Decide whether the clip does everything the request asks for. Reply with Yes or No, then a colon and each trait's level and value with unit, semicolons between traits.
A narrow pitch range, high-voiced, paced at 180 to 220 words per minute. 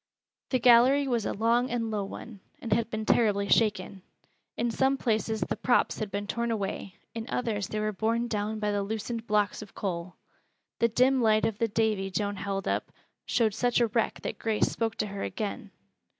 Yes: narrow, 2.3 semitones; high, 220 Hz; average, 195 wpm